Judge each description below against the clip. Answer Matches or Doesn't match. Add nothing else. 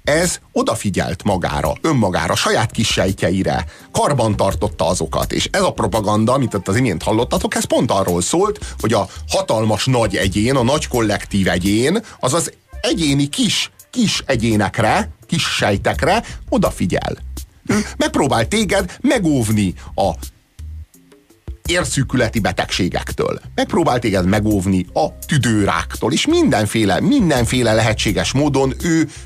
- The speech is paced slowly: Doesn't match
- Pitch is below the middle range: Matches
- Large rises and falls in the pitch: Matches